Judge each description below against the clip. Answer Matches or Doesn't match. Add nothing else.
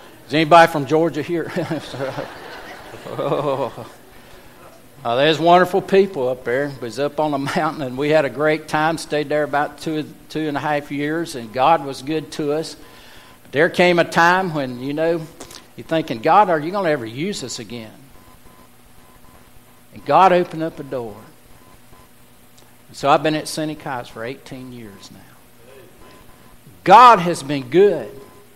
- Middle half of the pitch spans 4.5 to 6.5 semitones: Doesn't match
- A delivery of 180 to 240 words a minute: Doesn't match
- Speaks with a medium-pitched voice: Matches